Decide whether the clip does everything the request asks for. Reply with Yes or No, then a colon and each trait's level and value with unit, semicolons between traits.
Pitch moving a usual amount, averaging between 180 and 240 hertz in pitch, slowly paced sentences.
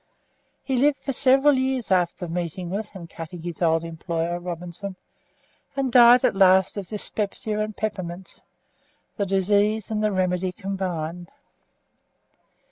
Yes: average, 3.7 semitones; high, 190 Hz; slow, 130 wpm